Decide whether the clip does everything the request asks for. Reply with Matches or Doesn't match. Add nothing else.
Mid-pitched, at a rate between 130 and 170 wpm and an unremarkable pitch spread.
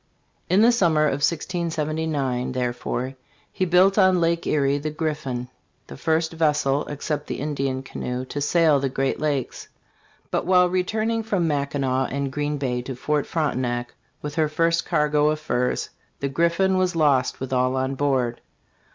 Matches